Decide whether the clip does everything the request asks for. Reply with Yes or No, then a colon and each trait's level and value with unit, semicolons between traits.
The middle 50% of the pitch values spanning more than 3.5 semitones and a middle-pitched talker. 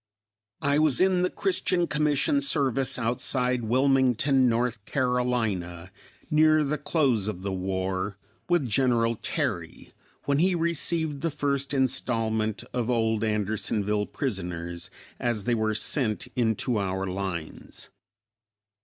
No: average, 5.2 semitones; low, 125 Hz